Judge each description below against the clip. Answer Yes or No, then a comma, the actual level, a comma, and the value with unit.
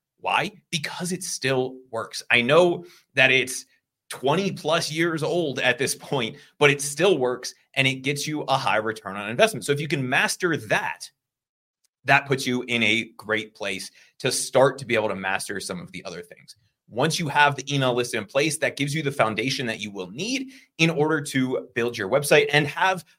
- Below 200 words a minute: No, fast, 205 wpm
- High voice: No, low, 135 Hz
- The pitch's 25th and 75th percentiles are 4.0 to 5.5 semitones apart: Yes, average, 4.3 semitones